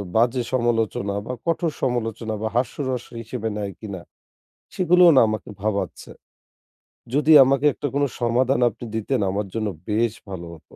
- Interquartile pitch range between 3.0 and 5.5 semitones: Yes, average, 3.4 semitones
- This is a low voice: Yes, low, 120 Hz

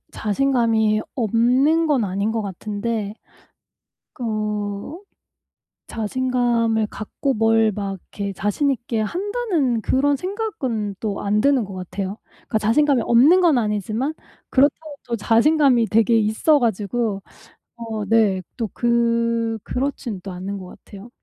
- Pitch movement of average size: Yes, average, 3.7 semitones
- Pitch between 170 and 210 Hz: No, high, 225 Hz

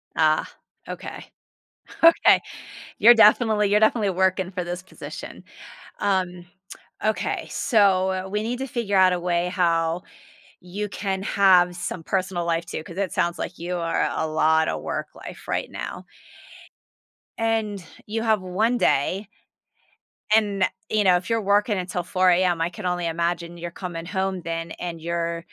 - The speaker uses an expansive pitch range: No, average, 3.0 semitones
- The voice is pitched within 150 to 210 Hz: Yes, medium, 185 Hz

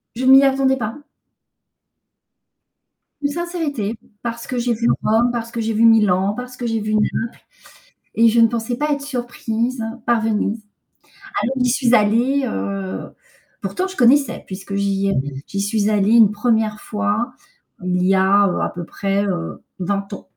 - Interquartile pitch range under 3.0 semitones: No, average, 3.7 semitones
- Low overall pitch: No, high, 225 Hz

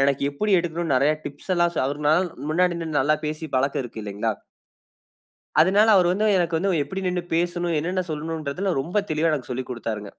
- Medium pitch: Yes, medium, 160 Hz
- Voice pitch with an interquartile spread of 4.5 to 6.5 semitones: No, average, 4.0 semitones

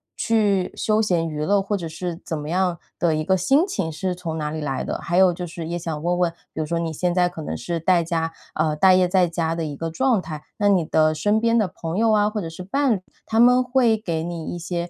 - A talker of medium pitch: Yes, medium, 175 Hz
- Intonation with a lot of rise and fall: No, average, 3.7 semitones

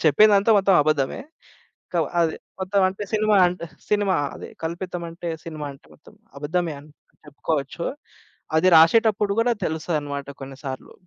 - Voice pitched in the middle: Yes, medium, 170 Hz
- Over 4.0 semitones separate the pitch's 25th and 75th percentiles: Yes, average, 5.1 semitones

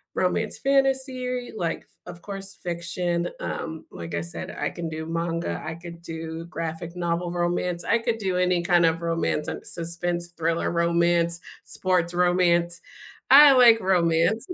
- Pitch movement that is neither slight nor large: No, narrow, 1.7 semitones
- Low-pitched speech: No, medium, 175 Hz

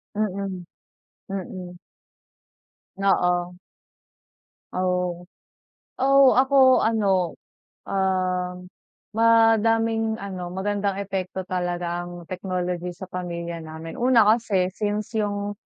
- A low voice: No, high, 190 Hz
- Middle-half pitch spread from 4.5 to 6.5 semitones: No, average, 3.2 semitones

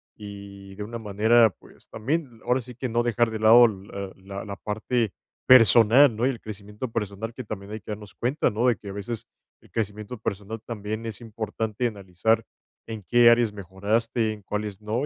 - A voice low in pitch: Yes, low, 110 Hz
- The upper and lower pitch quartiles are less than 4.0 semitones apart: Yes, narrow, 2.5 semitones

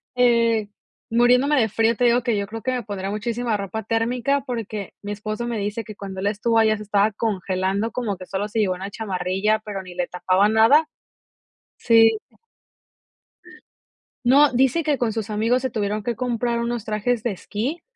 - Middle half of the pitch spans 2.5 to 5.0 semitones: Yes, average, 2.9 semitones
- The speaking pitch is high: Yes, high, 220 Hz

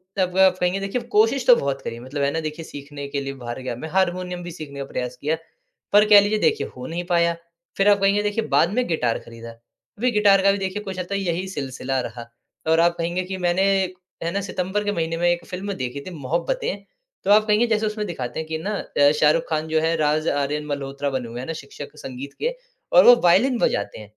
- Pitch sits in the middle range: Yes, medium, 170 Hz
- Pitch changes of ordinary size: No, wide, 5.8 semitones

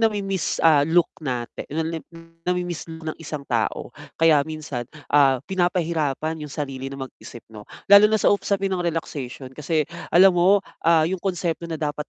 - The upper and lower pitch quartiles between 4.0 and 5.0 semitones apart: No, average, 3.5 semitones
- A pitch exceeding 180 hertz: No, medium, 160 Hz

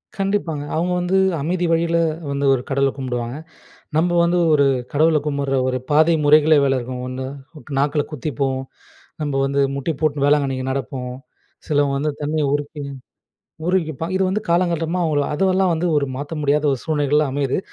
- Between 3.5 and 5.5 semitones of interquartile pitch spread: No, average, 3.1 semitones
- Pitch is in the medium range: Yes, medium, 145 Hz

